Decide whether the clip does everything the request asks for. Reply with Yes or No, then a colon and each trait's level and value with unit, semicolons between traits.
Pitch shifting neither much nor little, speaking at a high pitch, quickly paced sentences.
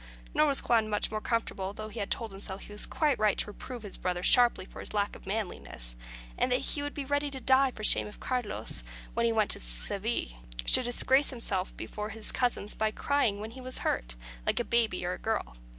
Yes: average, 3.9 semitones; high, 220 Hz; fast, 225 wpm